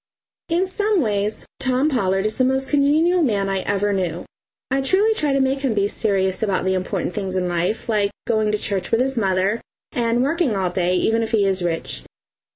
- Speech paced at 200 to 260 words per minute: Yes, fast, 205 wpm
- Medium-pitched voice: No, high, 215 Hz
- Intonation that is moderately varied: No, wide, 5.8 semitones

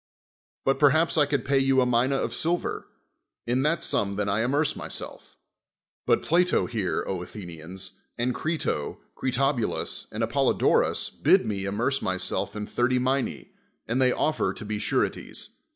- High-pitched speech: No, low, 125 Hz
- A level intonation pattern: No, average, 5.0 semitones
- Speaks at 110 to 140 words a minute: No, average, 155 wpm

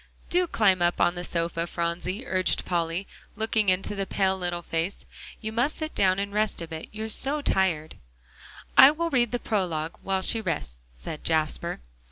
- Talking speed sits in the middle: Yes, average, 180 wpm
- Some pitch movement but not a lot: Yes, average, 4.4 semitones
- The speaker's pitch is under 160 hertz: No, medium, 185 Hz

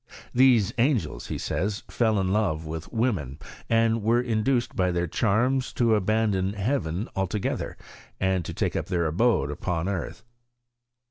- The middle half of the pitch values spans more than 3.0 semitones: Yes, average, 4.3 semitones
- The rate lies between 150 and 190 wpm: No, average, 140 wpm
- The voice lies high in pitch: No, low, 105 Hz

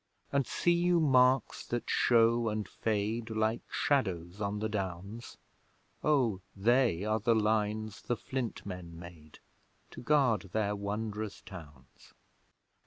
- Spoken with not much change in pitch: No, average, 3.2 semitones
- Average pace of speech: No, slow, 125 wpm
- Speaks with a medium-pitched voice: No, low, 110 Hz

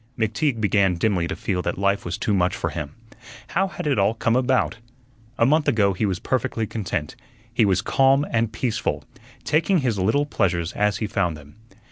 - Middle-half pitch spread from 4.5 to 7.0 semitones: Yes, average, 5.0 semitones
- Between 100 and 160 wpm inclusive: No, average, 190 wpm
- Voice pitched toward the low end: Yes, low, 105 Hz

